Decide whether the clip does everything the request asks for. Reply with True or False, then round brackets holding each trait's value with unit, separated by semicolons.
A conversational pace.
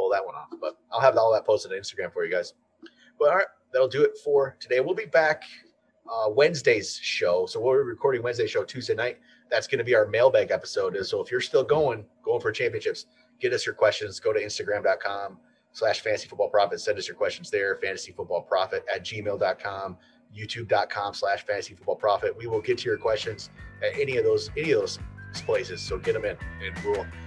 False (215 wpm)